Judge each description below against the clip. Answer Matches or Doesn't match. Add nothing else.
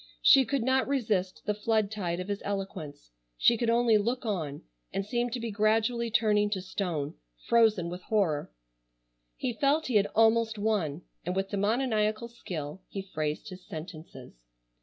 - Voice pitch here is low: Doesn't match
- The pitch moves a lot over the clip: Doesn't match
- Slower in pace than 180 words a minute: Matches